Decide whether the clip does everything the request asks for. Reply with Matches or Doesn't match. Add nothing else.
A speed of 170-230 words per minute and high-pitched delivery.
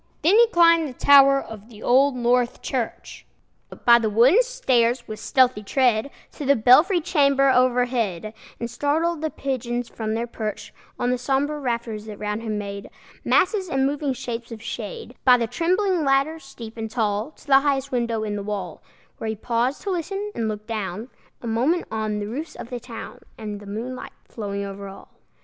Matches